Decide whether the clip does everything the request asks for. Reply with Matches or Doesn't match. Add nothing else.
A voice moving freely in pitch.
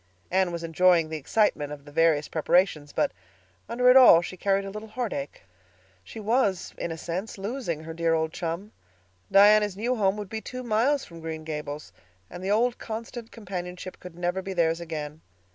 Doesn't match